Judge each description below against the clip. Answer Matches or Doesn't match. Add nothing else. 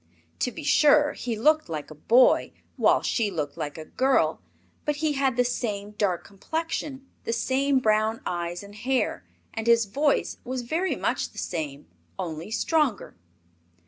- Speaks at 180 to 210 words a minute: Doesn't match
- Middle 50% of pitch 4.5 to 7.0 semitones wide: Matches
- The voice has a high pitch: Matches